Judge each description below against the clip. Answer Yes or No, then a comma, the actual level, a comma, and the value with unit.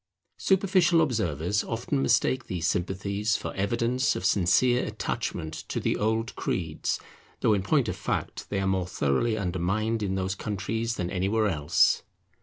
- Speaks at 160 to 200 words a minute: No, average, 150 wpm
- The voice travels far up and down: No, average, 3.7 semitones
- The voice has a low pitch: Yes, low, 105 Hz